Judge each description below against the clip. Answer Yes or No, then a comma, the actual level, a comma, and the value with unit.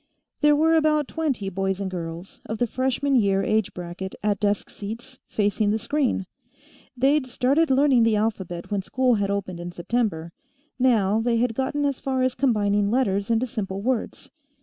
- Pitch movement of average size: Yes, average, 4.8 semitones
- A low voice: No, high, 225 Hz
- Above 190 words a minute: No, average, 170 wpm